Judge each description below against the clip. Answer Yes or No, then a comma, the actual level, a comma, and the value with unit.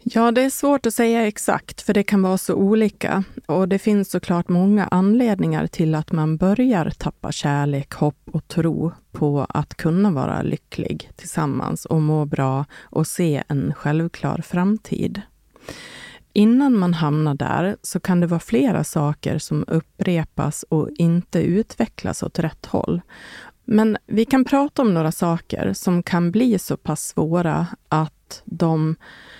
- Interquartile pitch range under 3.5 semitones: No, average, 5.0 semitones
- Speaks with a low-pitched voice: No, medium, 175 Hz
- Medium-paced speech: Yes, average, 155 wpm